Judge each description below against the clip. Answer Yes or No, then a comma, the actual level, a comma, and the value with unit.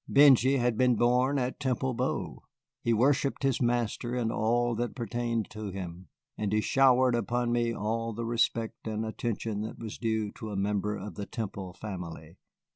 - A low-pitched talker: Yes, low, 115 Hz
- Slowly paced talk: No, average, 175 wpm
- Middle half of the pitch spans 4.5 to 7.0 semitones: No, narrow, 2.5 semitones